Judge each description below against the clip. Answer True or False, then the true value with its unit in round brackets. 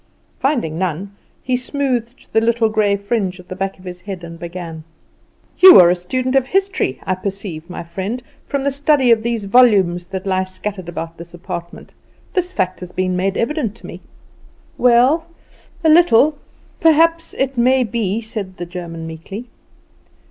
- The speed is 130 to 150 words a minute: False (170 wpm)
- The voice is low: False (200 Hz)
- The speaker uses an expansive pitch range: True (5.9 semitones)